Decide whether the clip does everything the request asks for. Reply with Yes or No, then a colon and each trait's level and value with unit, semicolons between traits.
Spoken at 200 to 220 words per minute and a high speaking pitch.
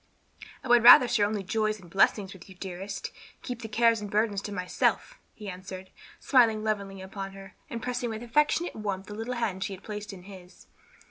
Yes: fast, 205 wpm; high, 210 Hz